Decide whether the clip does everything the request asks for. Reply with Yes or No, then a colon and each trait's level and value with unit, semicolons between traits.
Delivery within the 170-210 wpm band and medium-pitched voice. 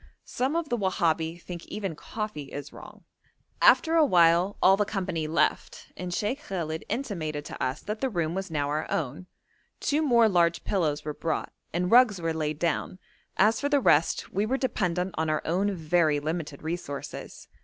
Yes: average, 175 wpm; medium, 175 Hz